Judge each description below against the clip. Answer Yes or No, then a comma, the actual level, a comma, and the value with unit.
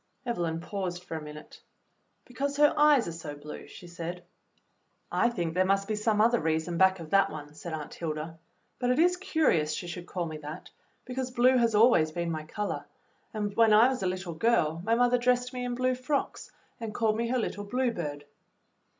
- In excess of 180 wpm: Yes, fast, 205 wpm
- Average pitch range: No, wide, 6.9 semitones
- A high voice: Yes, high, 200 Hz